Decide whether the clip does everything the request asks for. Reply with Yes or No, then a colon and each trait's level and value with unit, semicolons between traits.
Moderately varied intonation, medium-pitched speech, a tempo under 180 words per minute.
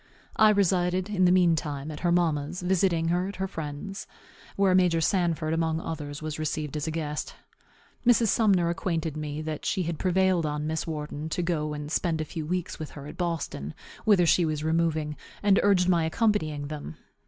No: average, 3.0 semitones; medium, 165 Hz; average, 190 wpm